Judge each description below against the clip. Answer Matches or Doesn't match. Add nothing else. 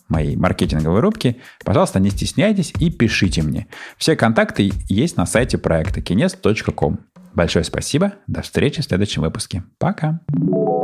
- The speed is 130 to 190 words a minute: Matches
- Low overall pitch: Matches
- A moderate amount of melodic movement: Doesn't match